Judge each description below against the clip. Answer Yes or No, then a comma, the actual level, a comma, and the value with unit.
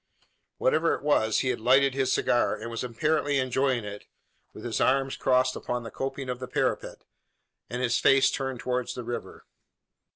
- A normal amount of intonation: No, narrow, 1.8 semitones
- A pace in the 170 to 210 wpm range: Yes, average, 175 wpm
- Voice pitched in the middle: No, low, 130 Hz